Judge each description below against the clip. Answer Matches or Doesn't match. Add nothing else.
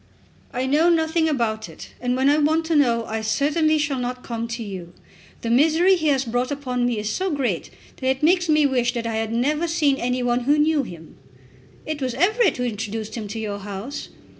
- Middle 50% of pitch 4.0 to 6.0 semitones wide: Matches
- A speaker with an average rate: Doesn't match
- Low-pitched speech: Doesn't match